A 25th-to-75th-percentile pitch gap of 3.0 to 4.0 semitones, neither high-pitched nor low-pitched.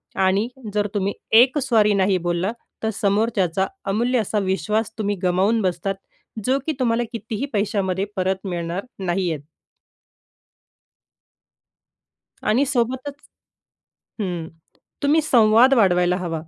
No: average, 3.7 semitones; high, 205 Hz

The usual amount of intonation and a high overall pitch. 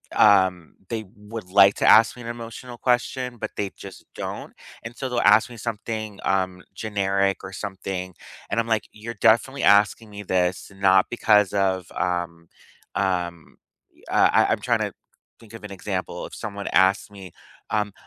No: average, 3.1 semitones; low, 105 Hz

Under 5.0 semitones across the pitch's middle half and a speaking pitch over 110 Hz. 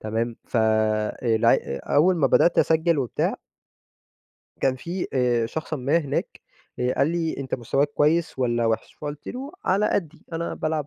No: wide, 5.6 semitones; medium, 140 Hz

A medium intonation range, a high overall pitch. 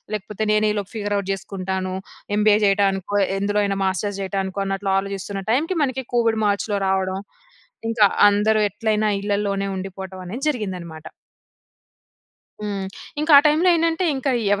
No: narrow, 2.1 semitones; high, 205 Hz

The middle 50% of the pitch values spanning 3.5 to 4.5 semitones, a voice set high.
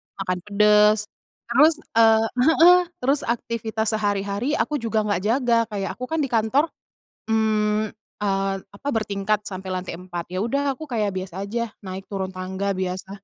No: average, 3.0 semitones; high, 210 Hz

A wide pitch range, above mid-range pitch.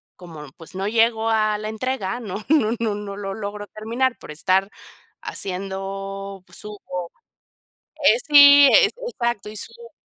No: average, 3.3 semitones; high, 210 Hz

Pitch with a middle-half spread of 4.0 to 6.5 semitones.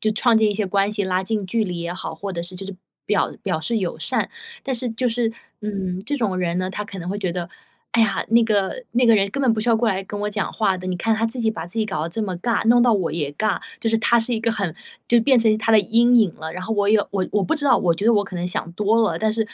No: average, 3.4 semitones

